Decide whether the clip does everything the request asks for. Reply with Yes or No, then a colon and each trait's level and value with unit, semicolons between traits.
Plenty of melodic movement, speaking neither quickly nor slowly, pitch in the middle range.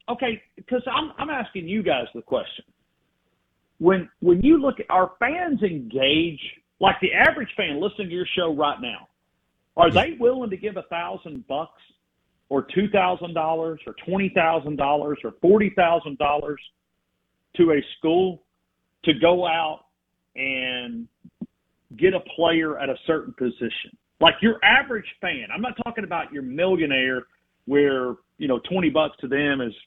Yes: wide, 5.9 semitones; average, 160 wpm; medium, 175 Hz